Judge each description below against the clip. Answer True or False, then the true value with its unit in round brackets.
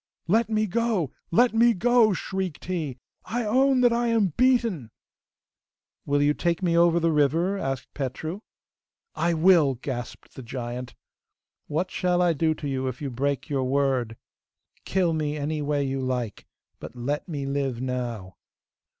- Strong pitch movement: True (6.1 semitones)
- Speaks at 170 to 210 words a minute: False (160 wpm)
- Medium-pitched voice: True (155 Hz)